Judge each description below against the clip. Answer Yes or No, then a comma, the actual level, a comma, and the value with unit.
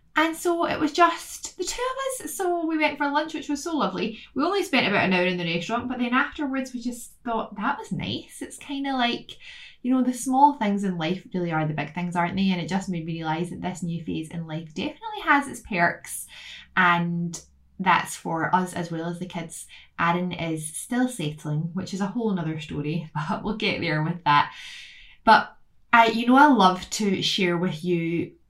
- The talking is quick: Yes, fast, 225 wpm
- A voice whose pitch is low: No, high, 200 Hz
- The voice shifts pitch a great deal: Yes, wide, 8.9 semitones